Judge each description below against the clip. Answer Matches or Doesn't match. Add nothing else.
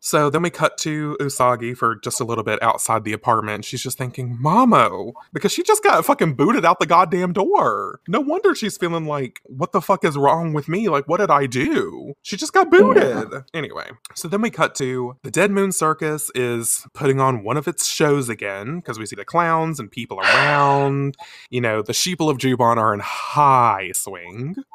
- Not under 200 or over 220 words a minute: Matches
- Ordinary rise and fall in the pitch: Doesn't match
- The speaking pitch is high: Doesn't match